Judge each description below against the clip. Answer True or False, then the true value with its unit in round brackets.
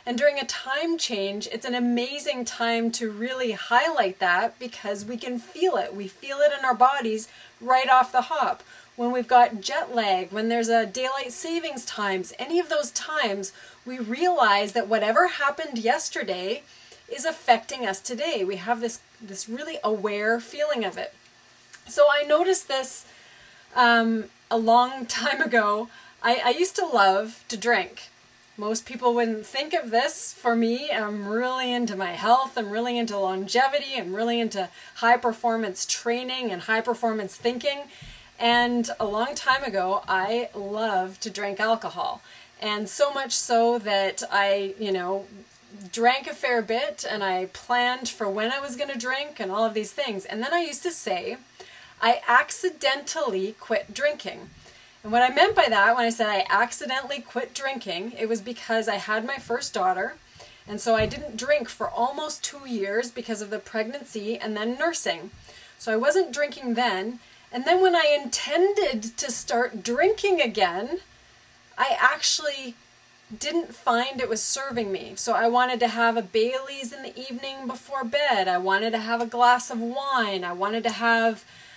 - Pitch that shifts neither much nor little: True (3.7 semitones)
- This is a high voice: True (240 Hz)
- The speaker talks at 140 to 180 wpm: True (170 wpm)